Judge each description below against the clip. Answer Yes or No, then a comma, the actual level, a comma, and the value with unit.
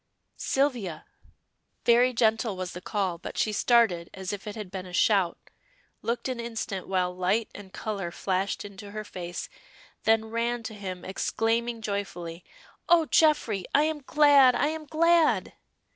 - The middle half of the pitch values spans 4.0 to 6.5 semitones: Yes, average, 4.3 semitones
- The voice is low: No, high, 215 Hz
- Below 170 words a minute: Yes, average, 155 wpm